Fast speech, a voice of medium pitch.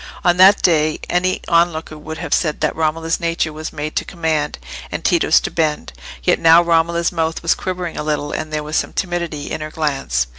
Yes: fast, 210 wpm; medium, 160 Hz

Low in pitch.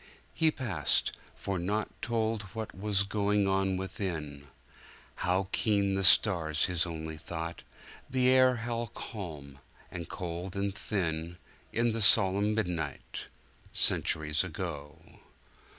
Yes: very low, 95 Hz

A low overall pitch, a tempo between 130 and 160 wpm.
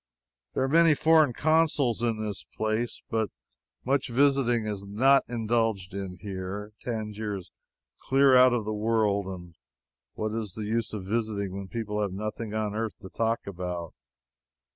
Yes: low, 110 Hz; average, 155 wpm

